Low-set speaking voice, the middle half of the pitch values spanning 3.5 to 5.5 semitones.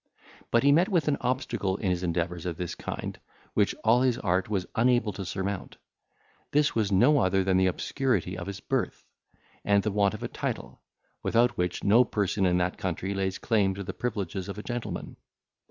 Yes: low, 100 Hz; average, 4.3 semitones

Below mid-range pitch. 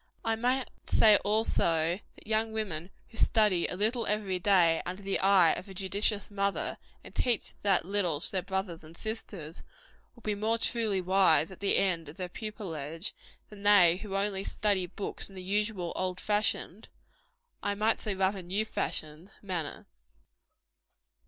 No: high, 195 Hz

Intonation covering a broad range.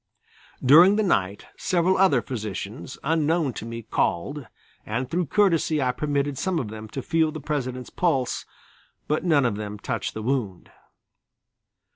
Yes: wide, 5.8 semitones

